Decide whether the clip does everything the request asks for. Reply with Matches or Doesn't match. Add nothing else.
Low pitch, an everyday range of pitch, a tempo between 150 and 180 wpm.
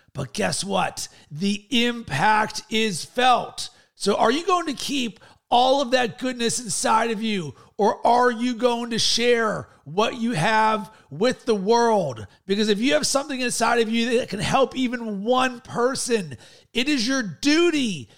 Doesn't match